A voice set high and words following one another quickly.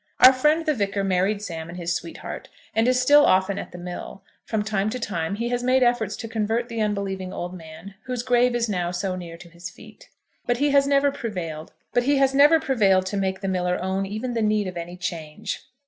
Yes: high, 205 Hz; fast, 210 wpm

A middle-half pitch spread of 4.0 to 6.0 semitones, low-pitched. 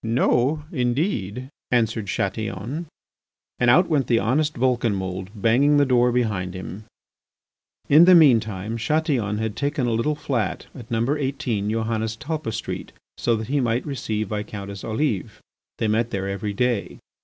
Yes: average, 4.4 semitones; low, 115 Hz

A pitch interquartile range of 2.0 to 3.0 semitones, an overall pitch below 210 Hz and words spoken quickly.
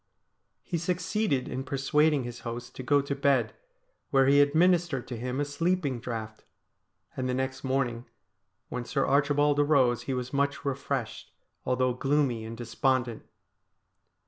No: narrow, 2.6 semitones; low, 135 Hz; average, 145 wpm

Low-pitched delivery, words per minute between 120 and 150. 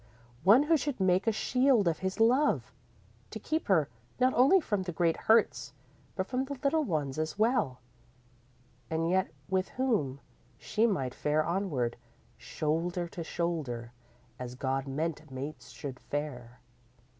No: medium, 175 Hz; average, 145 wpm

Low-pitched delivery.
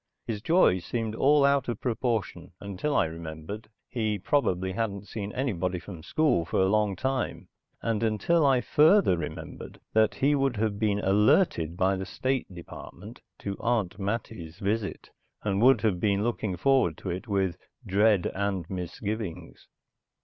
Yes: low, 105 Hz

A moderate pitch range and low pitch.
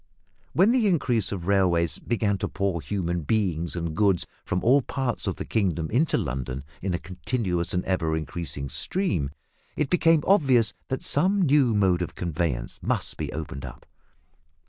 No: wide, 7.2 semitones; very low, 95 Hz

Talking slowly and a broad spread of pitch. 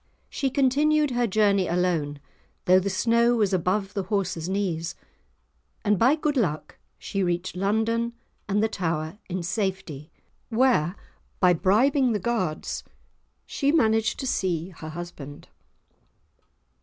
No: slow, 130 wpm; average, 5.0 semitones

